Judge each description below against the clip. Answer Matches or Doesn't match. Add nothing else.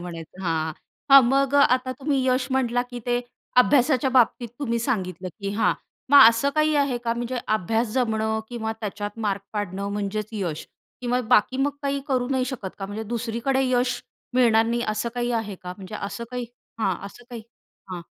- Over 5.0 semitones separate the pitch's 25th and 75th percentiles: Doesn't match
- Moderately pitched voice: Doesn't match